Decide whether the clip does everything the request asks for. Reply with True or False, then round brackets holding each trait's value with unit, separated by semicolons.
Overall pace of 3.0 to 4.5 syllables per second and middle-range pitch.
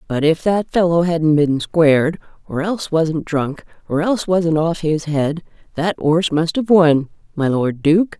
True (4.2 syllables/s; 165 Hz)